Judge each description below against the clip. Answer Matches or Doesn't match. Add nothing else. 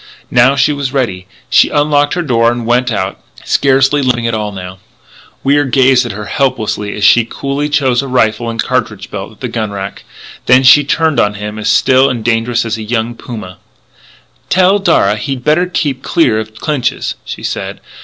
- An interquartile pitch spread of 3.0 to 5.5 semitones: Matches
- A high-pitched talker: Doesn't match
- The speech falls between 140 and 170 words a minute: Doesn't match